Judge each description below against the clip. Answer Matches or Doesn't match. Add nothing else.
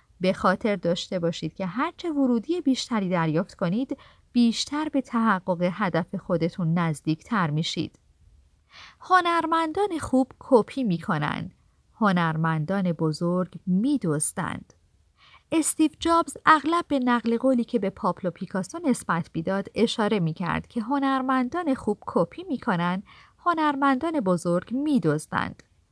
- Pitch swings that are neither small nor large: Doesn't match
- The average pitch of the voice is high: Matches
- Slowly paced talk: Doesn't match